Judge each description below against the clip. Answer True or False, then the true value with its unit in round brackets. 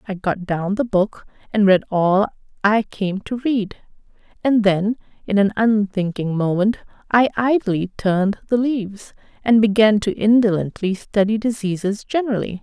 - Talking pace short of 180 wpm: True (145 wpm)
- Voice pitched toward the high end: True (210 Hz)